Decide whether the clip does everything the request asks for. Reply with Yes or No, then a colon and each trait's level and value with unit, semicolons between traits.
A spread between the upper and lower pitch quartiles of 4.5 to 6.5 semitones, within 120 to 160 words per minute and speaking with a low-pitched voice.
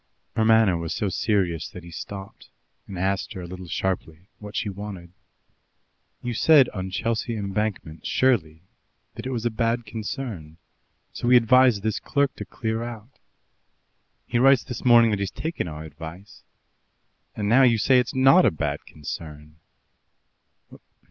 Yes: average, 5.2 semitones; average, 155 wpm; low, 105 Hz